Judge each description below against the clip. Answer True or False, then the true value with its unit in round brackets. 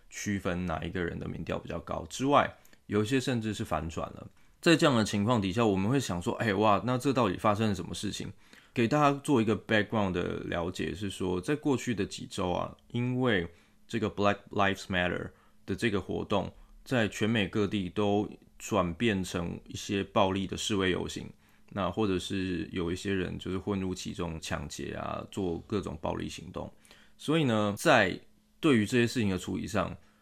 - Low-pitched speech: True (100 Hz)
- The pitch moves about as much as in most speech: True (3.7 semitones)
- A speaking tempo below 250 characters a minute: False (315 characters per minute)